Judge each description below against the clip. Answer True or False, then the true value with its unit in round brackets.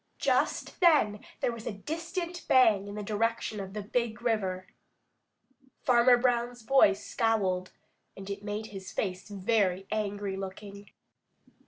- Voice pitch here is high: True (210 Hz)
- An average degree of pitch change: True (3.3 semitones)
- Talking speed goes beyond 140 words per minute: False (135 wpm)